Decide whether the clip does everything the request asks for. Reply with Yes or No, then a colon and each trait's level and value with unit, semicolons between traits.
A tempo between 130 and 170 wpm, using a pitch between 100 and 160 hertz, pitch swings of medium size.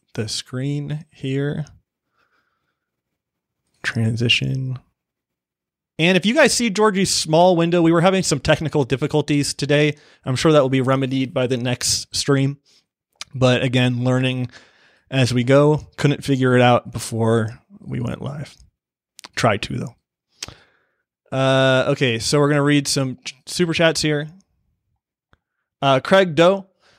Yes: slow, 135 wpm; medium, 140 Hz; average, 3.5 semitones